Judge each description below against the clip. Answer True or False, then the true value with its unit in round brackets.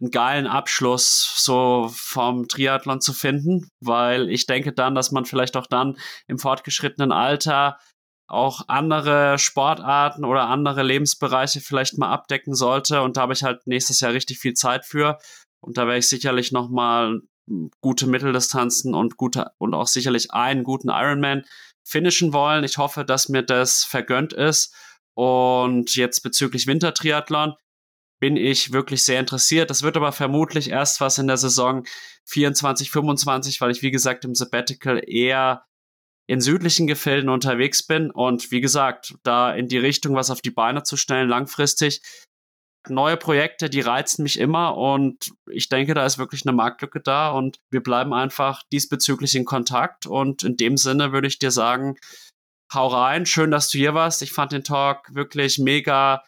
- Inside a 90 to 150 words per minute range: False (165 wpm)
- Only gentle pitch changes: True (2.2 semitones)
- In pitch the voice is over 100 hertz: True (135 Hz)